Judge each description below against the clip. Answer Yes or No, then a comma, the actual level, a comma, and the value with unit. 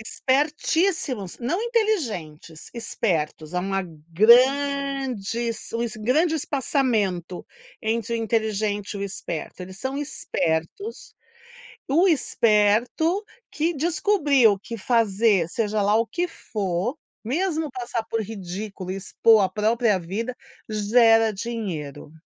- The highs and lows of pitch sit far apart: Yes, wide, 5.7 semitones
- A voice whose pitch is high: Yes, high, 225 Hz